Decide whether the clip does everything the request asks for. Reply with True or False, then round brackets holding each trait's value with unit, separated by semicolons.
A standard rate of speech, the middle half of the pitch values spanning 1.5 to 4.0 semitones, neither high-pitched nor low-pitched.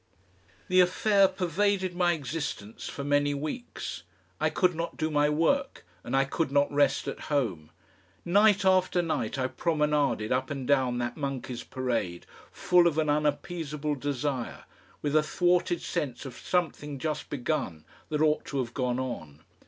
False (155 wpm; 4.7 semitones; 145 Hz)